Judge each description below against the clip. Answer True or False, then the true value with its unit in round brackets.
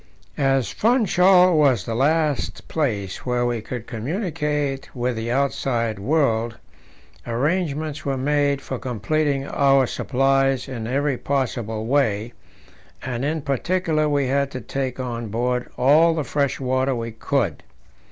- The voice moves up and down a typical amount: True (3.6 semitones)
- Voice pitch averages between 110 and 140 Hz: True (135 Hz)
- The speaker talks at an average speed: False (130 wpm)